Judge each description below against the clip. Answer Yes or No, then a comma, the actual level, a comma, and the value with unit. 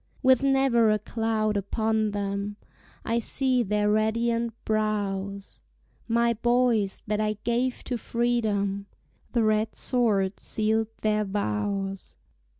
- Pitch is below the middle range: No, high, 215 Hz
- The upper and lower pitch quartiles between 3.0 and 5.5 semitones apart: No, narrow, 2.4 semitones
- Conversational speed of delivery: No, slow, 115 wpm